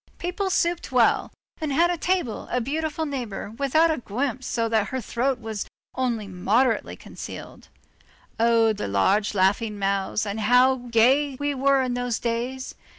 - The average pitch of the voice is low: No, high, 245 Hz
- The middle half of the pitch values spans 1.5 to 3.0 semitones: No, average, 4.0 semitones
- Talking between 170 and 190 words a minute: No, average, 155 wpm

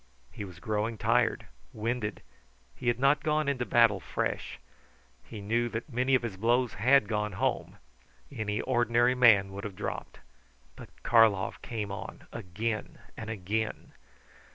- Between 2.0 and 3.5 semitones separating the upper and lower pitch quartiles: Yes, narrow, 2.6 semitones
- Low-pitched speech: Yes, low, 115 Hz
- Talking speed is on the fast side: No, average, 145 wpm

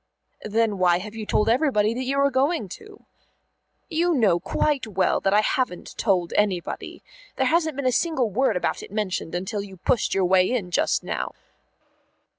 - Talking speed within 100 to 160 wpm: No, average, 175 wpm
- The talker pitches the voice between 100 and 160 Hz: No, high, 215 Hz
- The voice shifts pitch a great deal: Yes, wide, 5.9 semitones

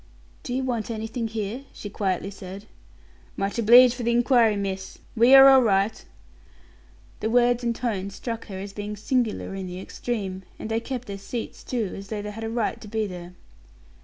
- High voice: Yes, high, 220 Hz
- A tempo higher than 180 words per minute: Yes, average, 190 wpm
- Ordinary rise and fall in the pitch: Yes, average, 3.4 semitones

